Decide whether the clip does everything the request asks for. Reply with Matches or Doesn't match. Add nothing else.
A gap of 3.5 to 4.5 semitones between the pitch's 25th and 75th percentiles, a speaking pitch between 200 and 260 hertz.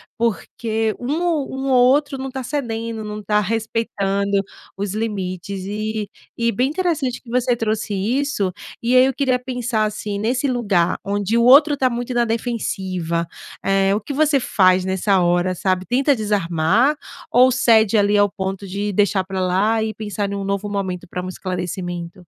Matches